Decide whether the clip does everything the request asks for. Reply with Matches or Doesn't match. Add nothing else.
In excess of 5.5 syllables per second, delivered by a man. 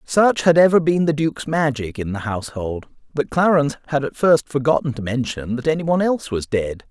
Matches